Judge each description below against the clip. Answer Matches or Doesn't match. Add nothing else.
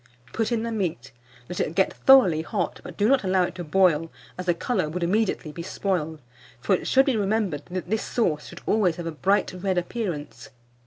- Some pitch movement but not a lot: Matches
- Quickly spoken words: Matches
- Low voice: Doesn't match